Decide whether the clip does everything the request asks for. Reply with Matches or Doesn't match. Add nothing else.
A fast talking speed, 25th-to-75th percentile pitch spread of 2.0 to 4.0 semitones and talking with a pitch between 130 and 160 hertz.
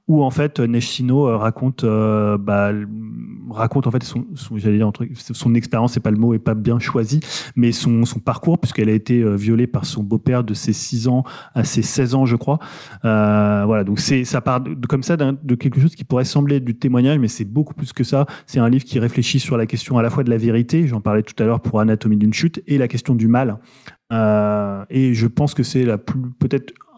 Doesn't match